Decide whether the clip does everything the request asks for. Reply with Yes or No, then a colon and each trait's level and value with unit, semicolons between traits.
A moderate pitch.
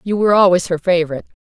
Yes: medium, 180 Hz